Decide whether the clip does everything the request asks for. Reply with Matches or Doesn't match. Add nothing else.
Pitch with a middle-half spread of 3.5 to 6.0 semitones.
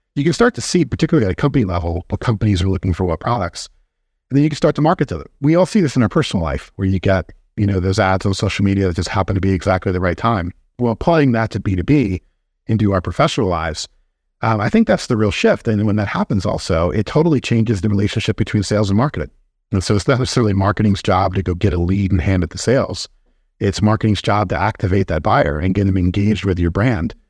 Matches